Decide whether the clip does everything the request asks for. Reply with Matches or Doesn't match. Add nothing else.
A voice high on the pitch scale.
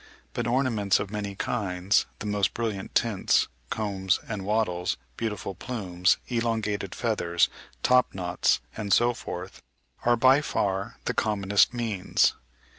Doesn't match